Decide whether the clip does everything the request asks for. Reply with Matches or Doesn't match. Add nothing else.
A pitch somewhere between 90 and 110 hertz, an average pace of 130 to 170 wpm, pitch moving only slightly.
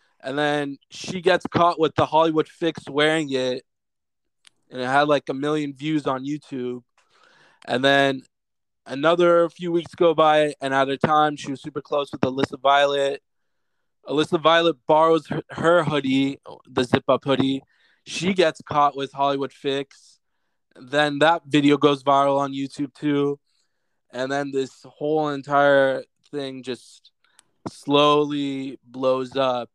Doesn't match